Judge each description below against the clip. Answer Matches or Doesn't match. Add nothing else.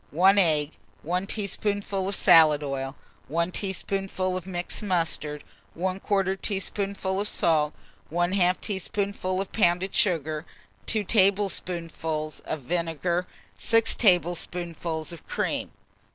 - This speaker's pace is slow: Matches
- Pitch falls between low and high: Matches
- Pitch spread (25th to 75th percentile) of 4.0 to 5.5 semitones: Doesn't match